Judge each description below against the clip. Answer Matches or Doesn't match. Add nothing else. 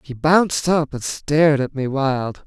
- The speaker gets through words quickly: Doesn't match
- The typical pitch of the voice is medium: Matches